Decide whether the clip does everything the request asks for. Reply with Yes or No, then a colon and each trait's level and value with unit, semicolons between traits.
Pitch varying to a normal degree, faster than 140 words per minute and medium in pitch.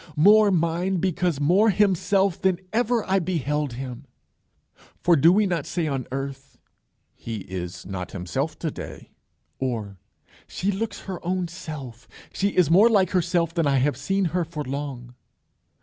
No: wide, 5.9 semitones; average, 155 wpm; medium, 165 Hz